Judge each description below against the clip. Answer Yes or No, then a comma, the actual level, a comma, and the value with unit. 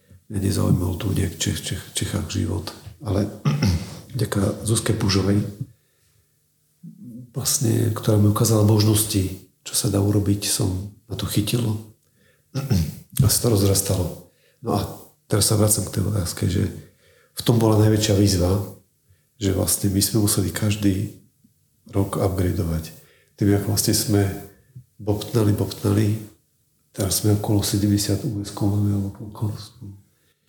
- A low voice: Yes, low, 105 Hz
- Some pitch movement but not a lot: No, narrow, 1.8 semitones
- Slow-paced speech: No, average, 125 wpm